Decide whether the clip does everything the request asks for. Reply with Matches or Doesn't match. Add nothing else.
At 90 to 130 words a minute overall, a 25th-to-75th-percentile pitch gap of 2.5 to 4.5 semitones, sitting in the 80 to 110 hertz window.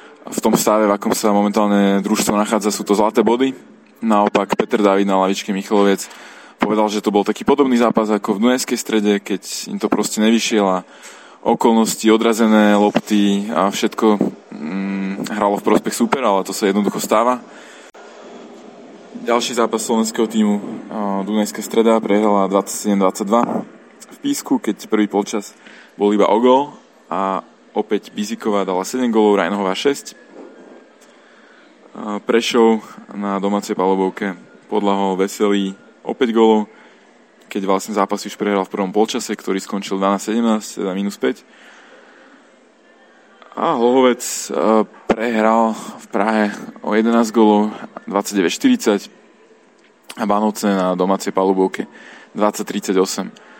Doesn't match